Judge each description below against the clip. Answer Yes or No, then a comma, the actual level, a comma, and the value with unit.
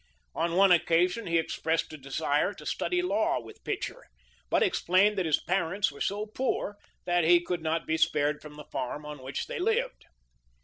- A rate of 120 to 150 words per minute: No, average, 185 wpm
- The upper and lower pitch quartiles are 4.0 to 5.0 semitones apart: Yes, average, 4.7 semitones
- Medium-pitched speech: Yes, medium, 170 Hz